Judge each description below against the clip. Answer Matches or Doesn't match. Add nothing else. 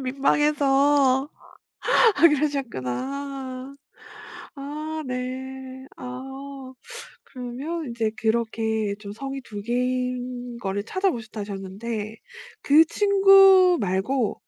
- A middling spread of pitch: Matches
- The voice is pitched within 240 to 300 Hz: Matches